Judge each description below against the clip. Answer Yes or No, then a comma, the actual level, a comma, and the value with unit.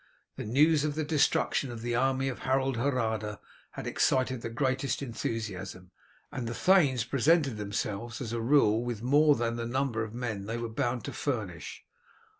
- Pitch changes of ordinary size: Yes, average, 3.3 semitones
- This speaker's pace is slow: No, average, 175 wpm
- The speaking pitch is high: No, low, 120 Hz